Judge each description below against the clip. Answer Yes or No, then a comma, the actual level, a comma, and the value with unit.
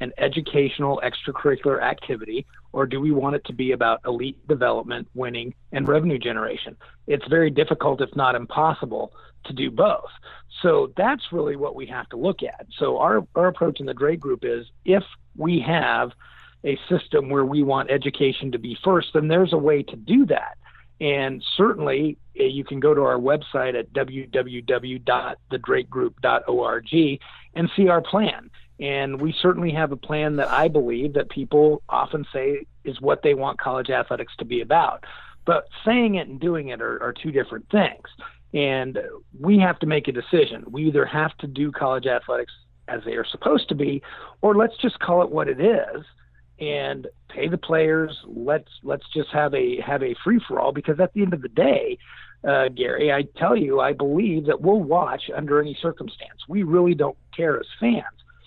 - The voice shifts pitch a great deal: No, average, 4.4 semitones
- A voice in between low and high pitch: Yes, medium, 150 Hz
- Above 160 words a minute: Yes, average, 185 wpm